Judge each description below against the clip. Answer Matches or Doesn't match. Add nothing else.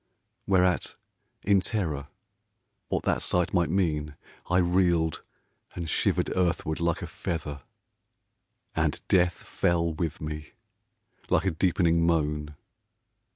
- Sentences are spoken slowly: Matches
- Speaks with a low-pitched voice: Matches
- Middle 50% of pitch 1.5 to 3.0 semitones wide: Matches